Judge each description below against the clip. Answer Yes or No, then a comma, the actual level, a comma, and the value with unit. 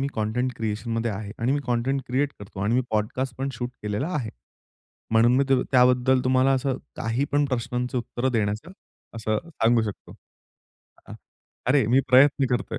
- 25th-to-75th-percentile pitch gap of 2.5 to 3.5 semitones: Yes, average, 2.9 semitones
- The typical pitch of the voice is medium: No, low, 125 Hz